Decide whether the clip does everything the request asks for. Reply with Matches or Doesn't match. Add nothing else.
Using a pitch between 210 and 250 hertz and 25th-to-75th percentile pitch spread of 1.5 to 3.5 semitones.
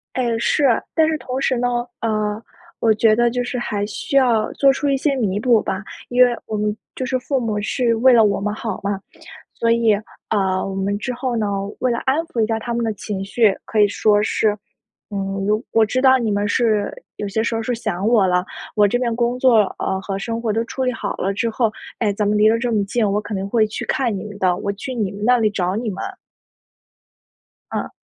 Matches